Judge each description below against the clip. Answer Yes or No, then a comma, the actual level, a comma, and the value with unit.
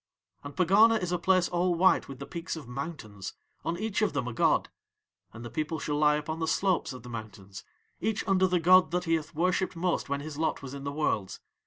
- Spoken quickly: Yes, fast, 230 wpm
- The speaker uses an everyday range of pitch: Yes, average, 4.5 semitones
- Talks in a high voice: No, medium, 160 Hz